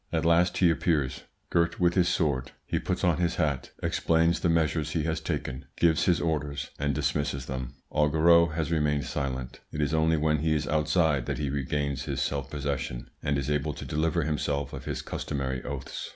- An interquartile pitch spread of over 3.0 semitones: No, narrow, 2.6 semitones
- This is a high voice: No, very low, 75 Hz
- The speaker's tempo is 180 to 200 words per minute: Yes, average, 195 wpm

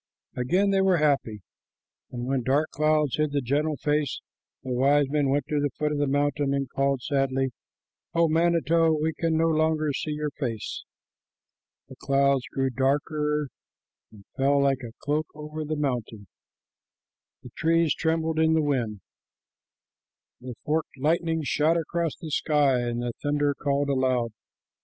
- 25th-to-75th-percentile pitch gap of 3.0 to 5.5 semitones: No, narrow, 2.6 semitones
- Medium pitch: Yes, medium, 145 Hz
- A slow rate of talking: No, average, 155 wpm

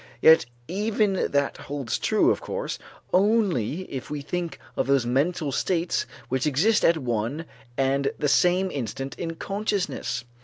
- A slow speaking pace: No, average, 145 wpm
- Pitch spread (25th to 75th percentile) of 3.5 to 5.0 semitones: No, wide, 5.4 semitones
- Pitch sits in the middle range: Yes, medium, 155 Hz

